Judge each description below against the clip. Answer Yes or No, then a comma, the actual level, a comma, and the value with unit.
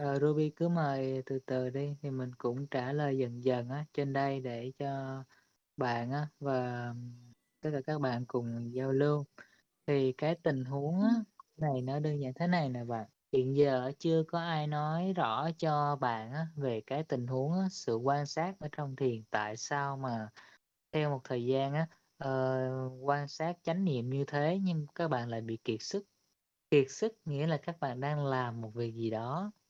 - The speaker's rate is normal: Yes, average, 195 wpm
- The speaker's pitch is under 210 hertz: Yes, medium, 140 Hz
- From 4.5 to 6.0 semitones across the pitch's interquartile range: No, average, 3.1 semitones